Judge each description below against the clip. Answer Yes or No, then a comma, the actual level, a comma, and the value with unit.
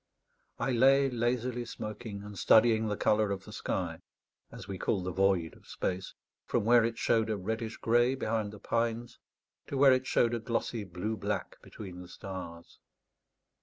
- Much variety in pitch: No, average, 3.3 semitones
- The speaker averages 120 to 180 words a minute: Yes, average, 170 wpm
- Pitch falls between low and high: No, low, 110 Hz